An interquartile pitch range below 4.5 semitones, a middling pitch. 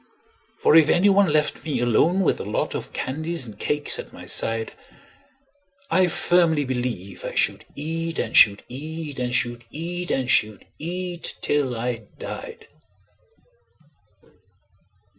No: wide, 5.6 semitones; medium, 150 Hz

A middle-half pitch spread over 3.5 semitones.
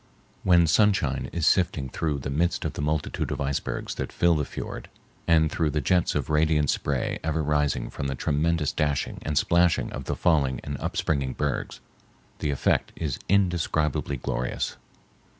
No: average, 2.9 semitones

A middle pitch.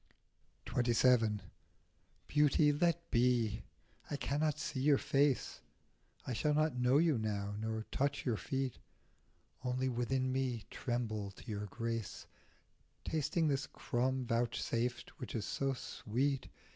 No: low, 125 Hz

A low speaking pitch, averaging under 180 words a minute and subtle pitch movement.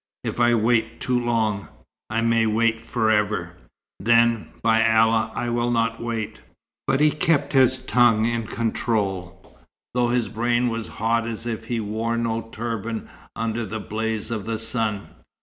Yes: low, 115 Hz; average, 160 wpm; narrow, 1.3 semitones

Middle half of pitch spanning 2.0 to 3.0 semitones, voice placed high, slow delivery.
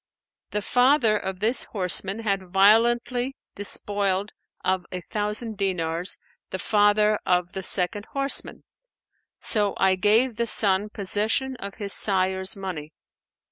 Yes: average, 2.7 semitones; high, 205 Hz; slow, 125 wpm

